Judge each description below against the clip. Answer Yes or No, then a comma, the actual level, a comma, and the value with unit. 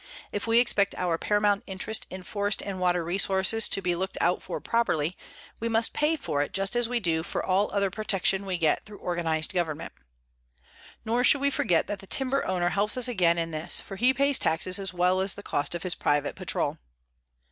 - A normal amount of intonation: Yes, average, 3.8 semitones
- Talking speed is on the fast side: Yes, fast, 210 wpm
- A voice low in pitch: No, high, 190 Hz